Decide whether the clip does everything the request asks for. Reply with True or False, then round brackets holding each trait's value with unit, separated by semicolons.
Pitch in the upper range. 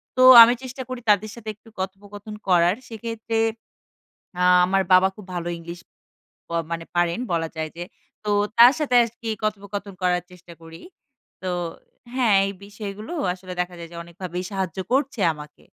True (195 Hz)